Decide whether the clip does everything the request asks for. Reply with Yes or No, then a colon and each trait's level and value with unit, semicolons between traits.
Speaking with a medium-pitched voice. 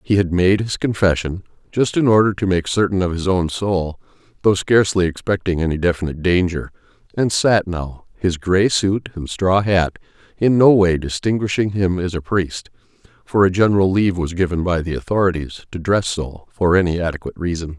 No: very low, 90 Hz